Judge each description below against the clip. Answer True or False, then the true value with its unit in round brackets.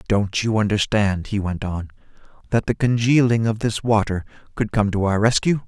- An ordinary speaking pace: True (180 wpm)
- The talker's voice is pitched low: True (105 Hz)